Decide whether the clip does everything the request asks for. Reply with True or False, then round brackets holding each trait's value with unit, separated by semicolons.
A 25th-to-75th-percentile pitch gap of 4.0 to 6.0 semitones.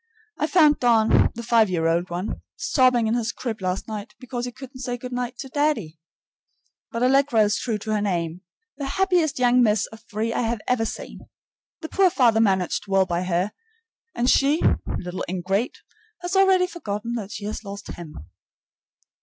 True (4.3 semitones)